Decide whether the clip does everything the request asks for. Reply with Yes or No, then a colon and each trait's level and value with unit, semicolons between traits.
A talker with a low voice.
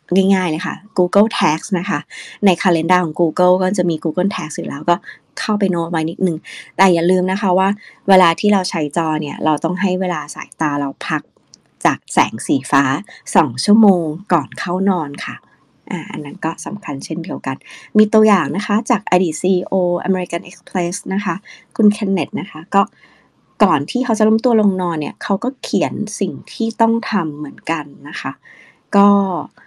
No: medium, 185 Hz